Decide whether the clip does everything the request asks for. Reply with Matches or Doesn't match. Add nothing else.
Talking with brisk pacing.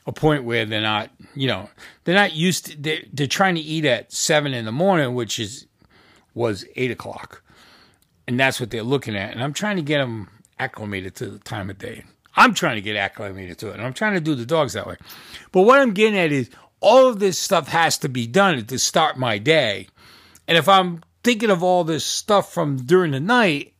Matches